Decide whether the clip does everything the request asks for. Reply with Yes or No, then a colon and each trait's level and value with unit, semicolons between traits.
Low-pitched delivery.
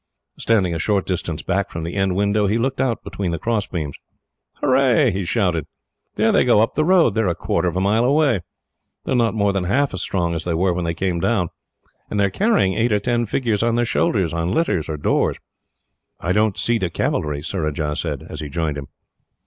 Yes: low, 100 Hz